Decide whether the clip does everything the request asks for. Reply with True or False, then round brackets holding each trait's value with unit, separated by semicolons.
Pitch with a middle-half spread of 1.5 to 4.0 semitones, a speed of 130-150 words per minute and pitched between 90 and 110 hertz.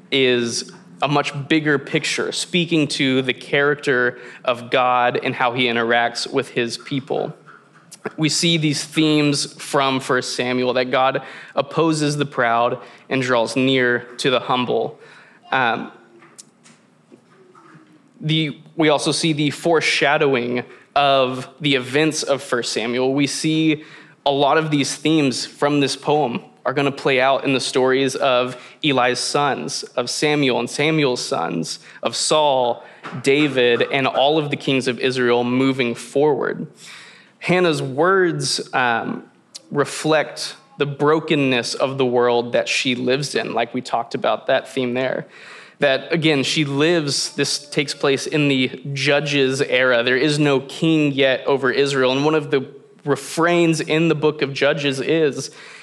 False (3.2 semitones; 145 wpm; 140 Hz)